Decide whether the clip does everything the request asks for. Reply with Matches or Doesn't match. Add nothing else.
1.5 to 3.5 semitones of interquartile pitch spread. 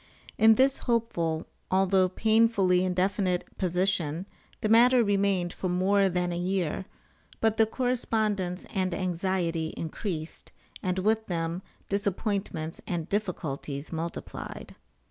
Matches